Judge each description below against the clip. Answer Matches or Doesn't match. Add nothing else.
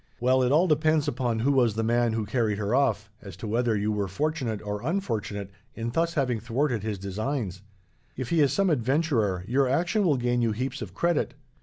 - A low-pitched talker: Matches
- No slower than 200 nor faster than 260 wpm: Matches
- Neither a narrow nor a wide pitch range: Matches